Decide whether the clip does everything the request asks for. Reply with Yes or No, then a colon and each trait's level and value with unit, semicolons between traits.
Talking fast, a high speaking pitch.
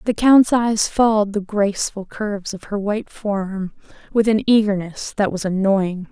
No: average, 165 wpm; high, 205 Hz